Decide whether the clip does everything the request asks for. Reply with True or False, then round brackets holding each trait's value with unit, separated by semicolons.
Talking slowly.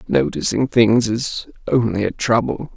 True (130 wpm)